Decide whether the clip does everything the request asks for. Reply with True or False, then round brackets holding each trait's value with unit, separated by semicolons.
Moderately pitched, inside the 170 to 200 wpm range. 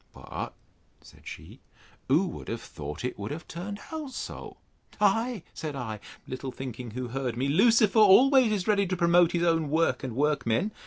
True (165 Hz; 175 wpm)